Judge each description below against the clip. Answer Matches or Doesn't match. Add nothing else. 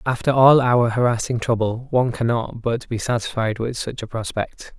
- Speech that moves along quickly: Doesn't match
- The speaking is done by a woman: Doesn't match